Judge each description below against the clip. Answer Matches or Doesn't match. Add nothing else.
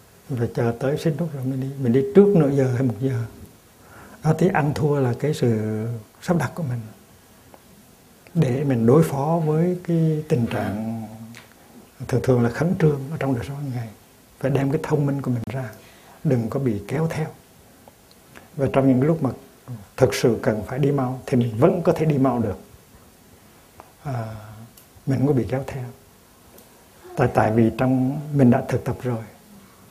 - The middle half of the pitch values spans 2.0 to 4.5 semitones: Matches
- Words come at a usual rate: Matches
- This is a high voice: Doesn't match